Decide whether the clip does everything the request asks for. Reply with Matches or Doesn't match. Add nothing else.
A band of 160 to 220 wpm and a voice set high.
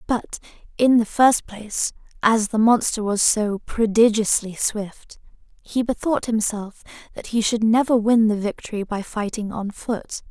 Doesn't match